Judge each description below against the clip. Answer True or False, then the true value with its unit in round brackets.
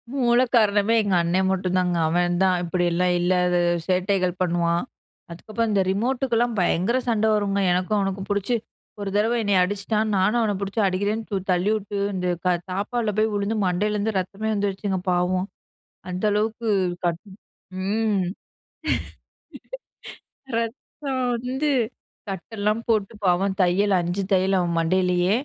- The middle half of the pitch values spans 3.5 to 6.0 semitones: False (3.1 semitones)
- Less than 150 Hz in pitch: False (200 Hz)